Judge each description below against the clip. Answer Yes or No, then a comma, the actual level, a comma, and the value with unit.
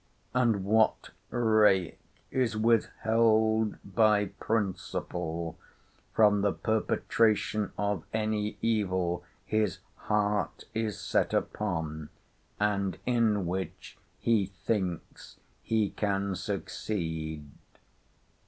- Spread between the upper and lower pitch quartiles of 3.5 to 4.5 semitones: No, average, 2.9 semitones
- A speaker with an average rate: No, slow, 85 wpm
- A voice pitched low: Yes, low, 105 Hz